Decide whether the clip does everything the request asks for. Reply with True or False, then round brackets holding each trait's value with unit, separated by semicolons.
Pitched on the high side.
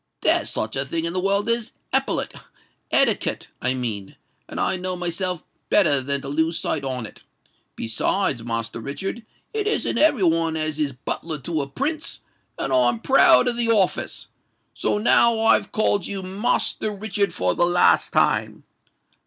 False (170 Hz)